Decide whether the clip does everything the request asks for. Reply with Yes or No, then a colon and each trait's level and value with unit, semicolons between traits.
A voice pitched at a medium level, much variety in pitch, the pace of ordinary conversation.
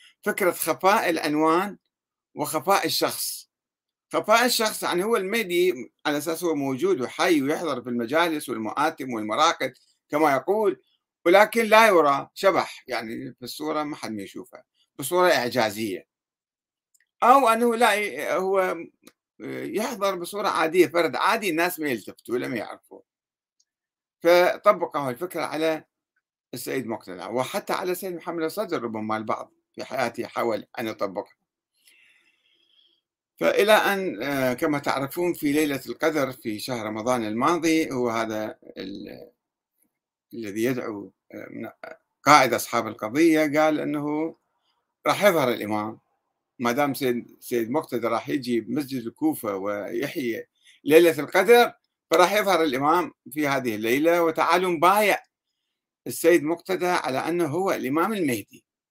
Yes: medium, 160 Hz; wide, 6.7 semitones; average, 120 wpm